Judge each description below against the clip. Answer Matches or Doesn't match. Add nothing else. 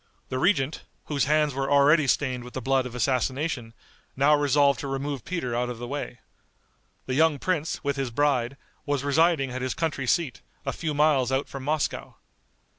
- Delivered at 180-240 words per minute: Matches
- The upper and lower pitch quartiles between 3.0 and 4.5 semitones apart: Doesn't match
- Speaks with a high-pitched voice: Doesn't match